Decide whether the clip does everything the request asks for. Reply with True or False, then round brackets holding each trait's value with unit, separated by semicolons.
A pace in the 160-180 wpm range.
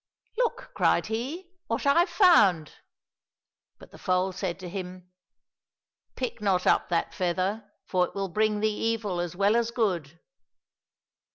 True (165 wpm)